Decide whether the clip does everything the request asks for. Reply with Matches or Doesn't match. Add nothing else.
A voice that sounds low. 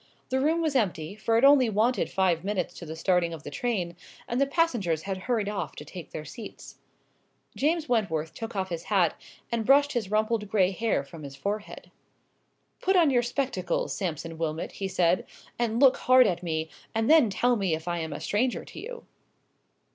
Doesn't match